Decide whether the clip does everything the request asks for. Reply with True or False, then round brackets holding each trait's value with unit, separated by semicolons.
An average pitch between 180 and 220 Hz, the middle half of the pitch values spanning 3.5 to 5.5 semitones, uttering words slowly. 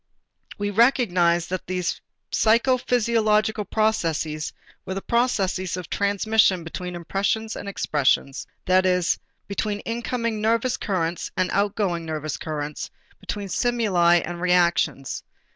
True (190 Hz; 4.1 semitones; 110 wpm)